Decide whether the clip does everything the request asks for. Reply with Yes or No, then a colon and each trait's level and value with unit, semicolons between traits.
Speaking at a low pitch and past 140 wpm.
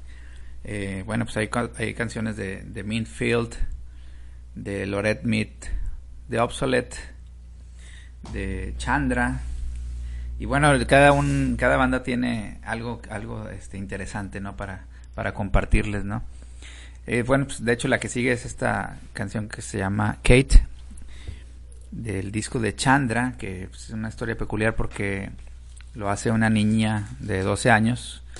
No: low, 100 Hz; average, 135 wpm